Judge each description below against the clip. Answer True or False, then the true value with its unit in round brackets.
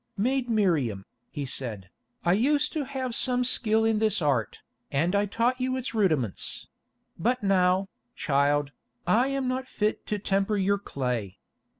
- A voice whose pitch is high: True (200 Hz)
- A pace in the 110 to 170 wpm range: True (155 wpm)